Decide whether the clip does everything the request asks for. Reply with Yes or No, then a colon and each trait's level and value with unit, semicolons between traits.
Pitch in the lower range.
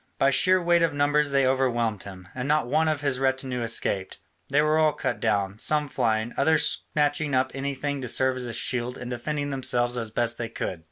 Yes: low, 130 Hz